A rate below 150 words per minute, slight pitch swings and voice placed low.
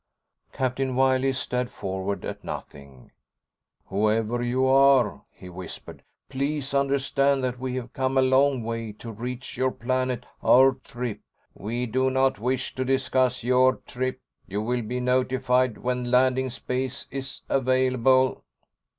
Yes: slow, 135 wpm; narrow, 1.5 semitones; low, 130 Hz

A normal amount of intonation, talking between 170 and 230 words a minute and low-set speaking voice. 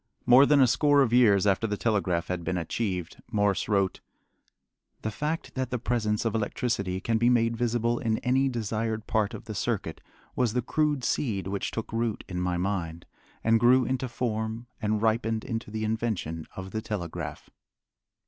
Yes: average, 3.4 semitones; average, 175 wpm; low, 110 Hz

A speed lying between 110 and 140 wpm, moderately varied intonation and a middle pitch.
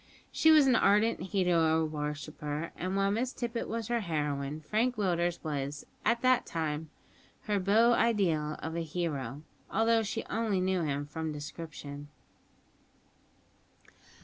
No: slow, 135 wpm; wide, 6.5 semitones; medium, 170 Hz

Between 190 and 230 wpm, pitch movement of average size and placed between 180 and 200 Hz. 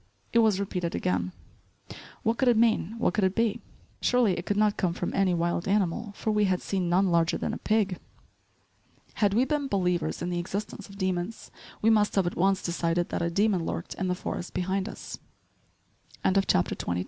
Yes: average, 195 wpm; average, 3.3 semitones; high, 190 Hz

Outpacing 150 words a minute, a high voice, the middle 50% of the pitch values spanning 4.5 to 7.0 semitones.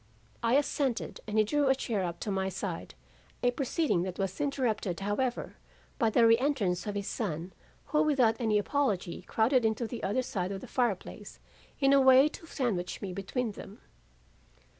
Yes: average, 180 wpm; high, 225 Hz; average, 5.2 semitones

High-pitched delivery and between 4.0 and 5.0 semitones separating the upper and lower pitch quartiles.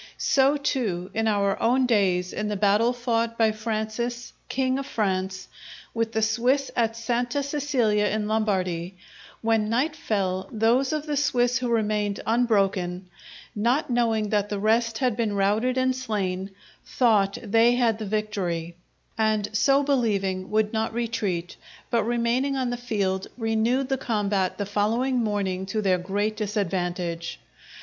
No: high, 220 Hz; average, 3.3 semitones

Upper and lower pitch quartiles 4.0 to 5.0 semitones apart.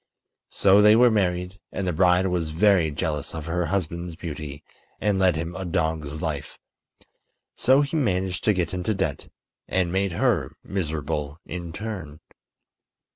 No: average, 3.4 semitones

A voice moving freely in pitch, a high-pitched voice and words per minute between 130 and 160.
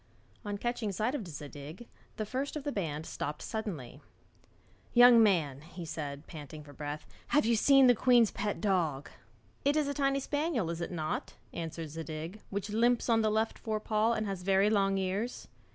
No: wide, 6.6 semitones; high, 200 Hz; average, 185 wpm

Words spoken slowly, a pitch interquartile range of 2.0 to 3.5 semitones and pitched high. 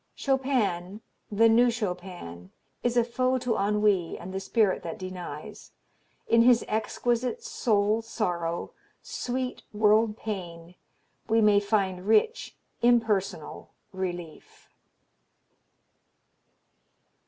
No: slow, 95 wpm; average, 4.3 semitones; high, 210 Hz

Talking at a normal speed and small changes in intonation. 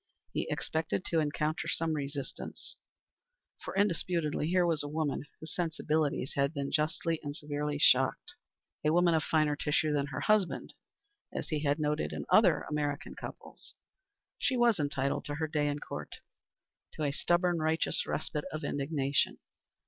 Yes: average, 155 wpm; narrow, 2.2 semitones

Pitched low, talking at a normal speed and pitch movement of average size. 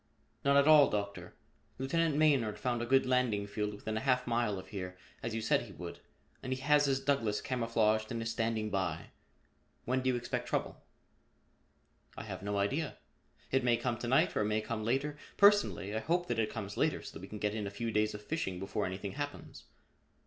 No: low, 115 Hz; fast, 215 wpm; average, 4.1 semitones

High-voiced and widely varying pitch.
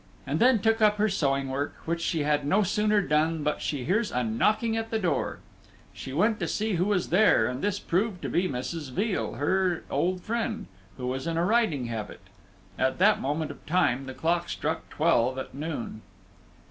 No: medium, 170 Hz; wide, 6.8 semitones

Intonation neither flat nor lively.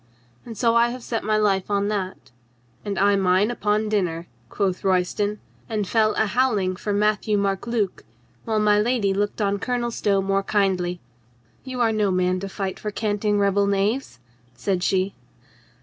No: narrow, 1.9 semitones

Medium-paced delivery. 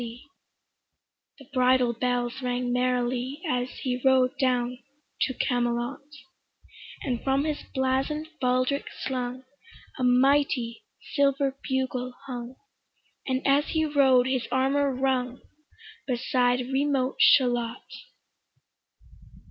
No: slow, 100 wpm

